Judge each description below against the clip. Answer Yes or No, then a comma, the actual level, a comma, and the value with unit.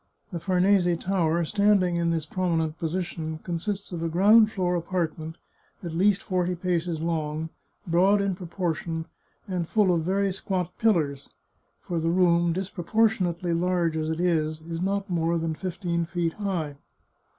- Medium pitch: Yes, medium, 175 Hz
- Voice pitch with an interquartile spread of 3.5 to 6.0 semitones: No, narrow, 2.4 semitones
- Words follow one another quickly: No, average, 150 wpm